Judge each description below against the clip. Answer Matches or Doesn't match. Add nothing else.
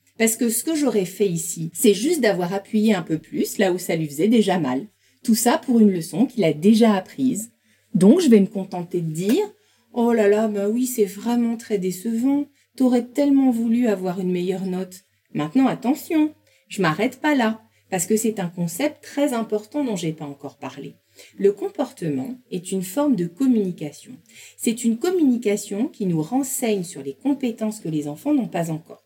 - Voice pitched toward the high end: Matches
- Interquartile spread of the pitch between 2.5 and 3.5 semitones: Doesn't match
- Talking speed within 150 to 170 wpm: Doesn't match